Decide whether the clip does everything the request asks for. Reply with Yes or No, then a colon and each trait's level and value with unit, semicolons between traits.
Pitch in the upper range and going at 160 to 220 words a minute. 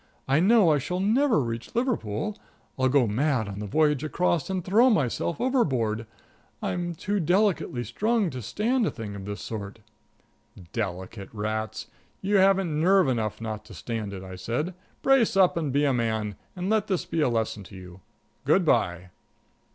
No: medium, 140 Hz; average, 175 wpm